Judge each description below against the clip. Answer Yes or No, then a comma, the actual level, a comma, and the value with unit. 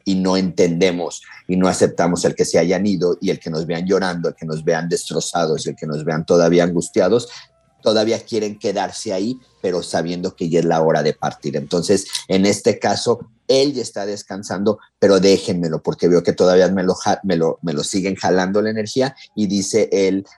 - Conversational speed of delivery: No, fast, 200 wpm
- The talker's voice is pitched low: Yes, very low, 95 Hz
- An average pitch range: Yes, average, 3.1 semitones